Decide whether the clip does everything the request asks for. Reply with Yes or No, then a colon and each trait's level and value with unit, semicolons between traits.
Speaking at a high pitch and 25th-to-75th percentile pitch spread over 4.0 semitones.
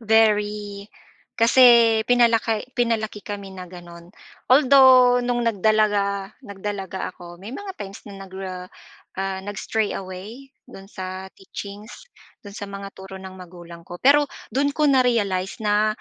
No: high, 205 Hz; average, 3.4 semitones